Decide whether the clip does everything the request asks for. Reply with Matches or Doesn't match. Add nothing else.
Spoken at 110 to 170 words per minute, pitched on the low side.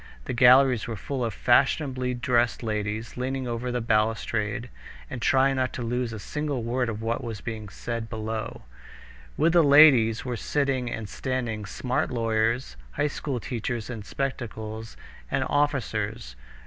Matches